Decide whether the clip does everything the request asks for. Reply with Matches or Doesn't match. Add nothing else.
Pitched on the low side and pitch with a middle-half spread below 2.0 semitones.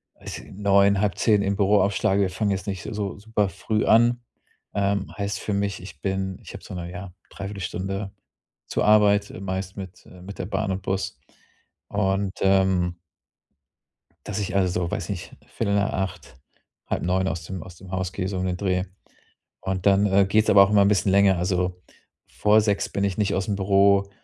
Matches